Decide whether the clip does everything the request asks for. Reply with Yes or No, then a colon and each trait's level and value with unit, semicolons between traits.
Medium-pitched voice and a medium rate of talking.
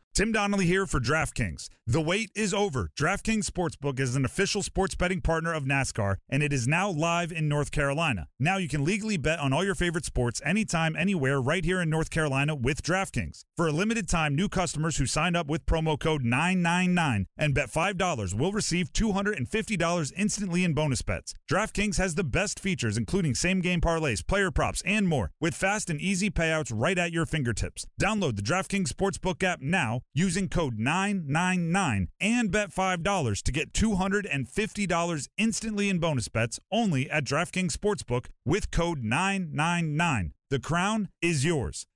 Yes: medium, 170 Hz; average, 175 wpm